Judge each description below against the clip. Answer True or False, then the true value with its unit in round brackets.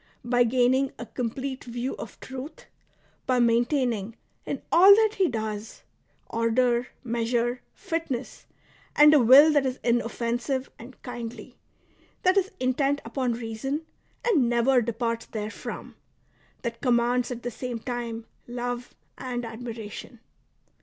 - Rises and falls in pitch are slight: True (2.1 semitones)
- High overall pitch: True (245 Hz)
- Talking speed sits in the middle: False (125 wpm)